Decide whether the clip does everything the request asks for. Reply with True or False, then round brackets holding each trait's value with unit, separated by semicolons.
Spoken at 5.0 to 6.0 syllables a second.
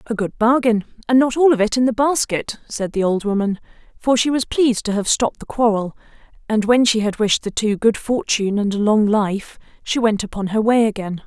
True (5.5 syllables/s)